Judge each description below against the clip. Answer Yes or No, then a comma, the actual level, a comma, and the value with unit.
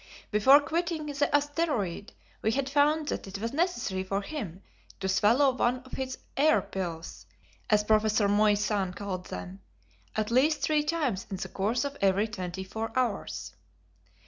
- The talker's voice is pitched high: Yes, high, 220 Hz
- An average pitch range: No, wide, 6.6 semitones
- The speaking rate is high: No, average, 155 wpm